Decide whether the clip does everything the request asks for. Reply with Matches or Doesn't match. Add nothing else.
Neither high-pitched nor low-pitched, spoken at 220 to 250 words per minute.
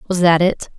Matches